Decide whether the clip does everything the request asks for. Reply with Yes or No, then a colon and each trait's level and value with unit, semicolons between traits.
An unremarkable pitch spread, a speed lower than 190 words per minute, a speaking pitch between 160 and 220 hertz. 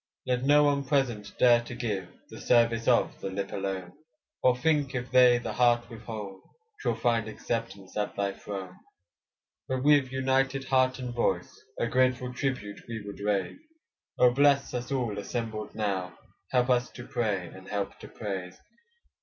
No: average, 4.0 semitones; average, 160 wpm; low, 120 Hz